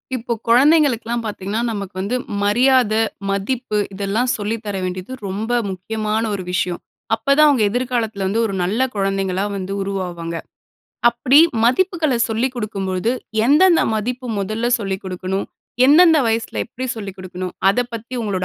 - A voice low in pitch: No, high, 215 Hz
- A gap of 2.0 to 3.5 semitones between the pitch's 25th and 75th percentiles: No, average, 4.2 semitones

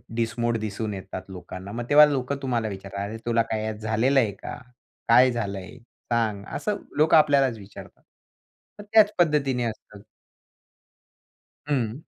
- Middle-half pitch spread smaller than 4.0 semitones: No, average, 4.3 semitones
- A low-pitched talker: Yes, low, 115 Hz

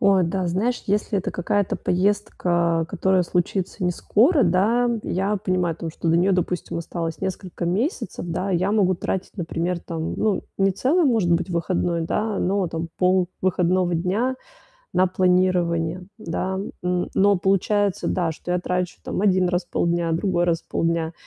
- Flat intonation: Yes, narrow, 2.3 semitones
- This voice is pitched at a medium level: Yes, medium, 180 Hz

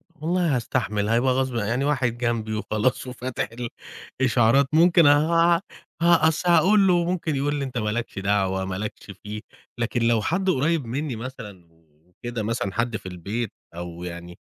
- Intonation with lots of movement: Yes, wide, 6.0 semitones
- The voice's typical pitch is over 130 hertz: No, low, 120 Hz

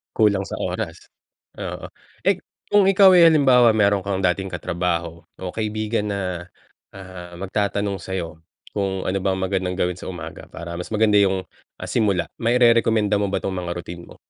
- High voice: No, very low, 95 Hz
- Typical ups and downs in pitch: Yes, average, 3.1 semitones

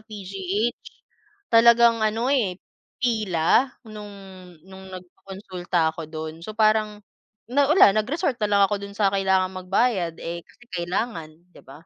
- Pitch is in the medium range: No, high, 200 Hz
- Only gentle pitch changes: No, average, 3.6 semitones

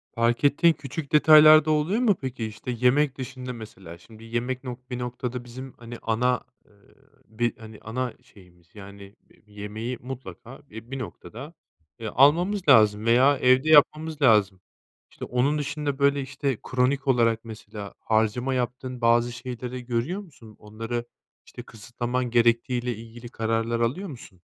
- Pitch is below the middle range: Yes, low, 125 Hz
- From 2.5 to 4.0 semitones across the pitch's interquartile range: Yes, average, 3.1 semitones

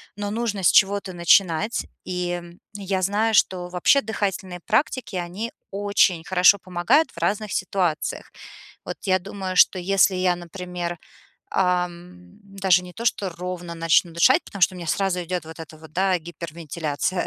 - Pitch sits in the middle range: Yes, medium, 180 Hz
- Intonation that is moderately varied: No, narrow, 2.3 semitones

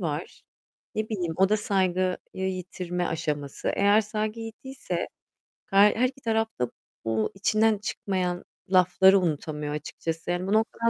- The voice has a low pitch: No, high, 190 Hz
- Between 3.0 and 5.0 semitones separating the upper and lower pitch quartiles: Yes, average, 3.7 semitones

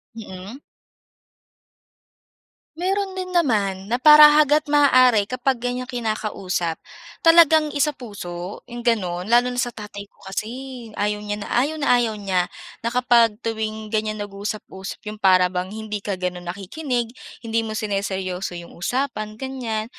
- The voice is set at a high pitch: Yes, high, 220 Hz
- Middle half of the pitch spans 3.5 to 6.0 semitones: Yes, average, 4.1 semitones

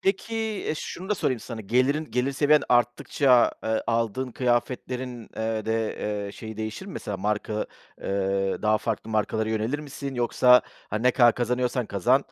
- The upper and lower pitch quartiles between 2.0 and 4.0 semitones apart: Yes, average, 3.0 semitones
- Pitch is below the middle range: Yes, low, 120 Hz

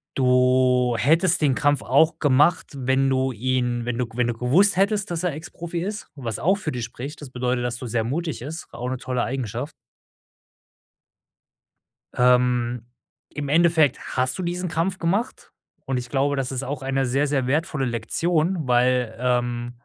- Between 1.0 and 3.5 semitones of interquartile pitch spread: No, average, 4.4 semitones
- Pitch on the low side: Yes, low, 130 Hz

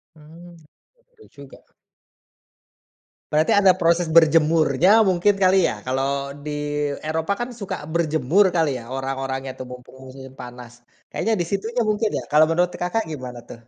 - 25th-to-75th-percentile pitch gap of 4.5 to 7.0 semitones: Yes, wide, 5.5 semitones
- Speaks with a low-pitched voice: No, medium, 160 Hz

